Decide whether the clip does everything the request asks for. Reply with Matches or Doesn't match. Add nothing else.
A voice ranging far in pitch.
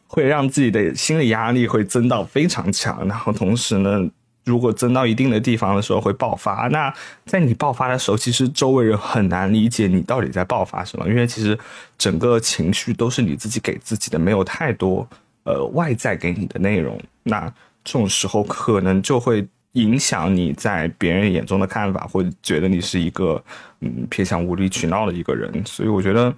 Doesn't match